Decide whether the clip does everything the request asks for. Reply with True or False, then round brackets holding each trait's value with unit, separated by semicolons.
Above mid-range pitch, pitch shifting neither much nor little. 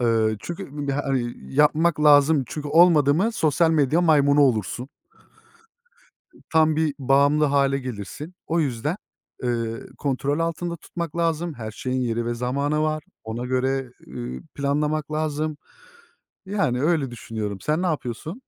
False (145 Hz; 4.0 semitones)